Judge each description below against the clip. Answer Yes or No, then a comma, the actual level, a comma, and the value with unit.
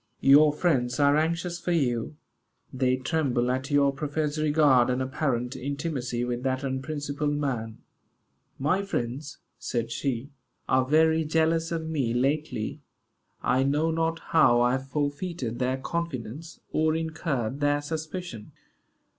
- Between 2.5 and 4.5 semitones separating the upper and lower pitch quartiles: Yes, average, 3.7 semitones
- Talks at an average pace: No, slow, 130 wpm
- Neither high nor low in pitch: Yes, medium, 145 Hz